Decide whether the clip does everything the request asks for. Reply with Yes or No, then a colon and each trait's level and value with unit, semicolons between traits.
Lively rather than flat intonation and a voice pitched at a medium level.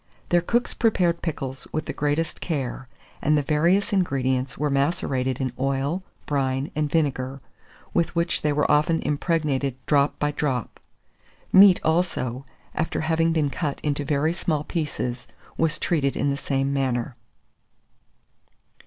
No: average, 3.3 semitones; medium, 145 Hz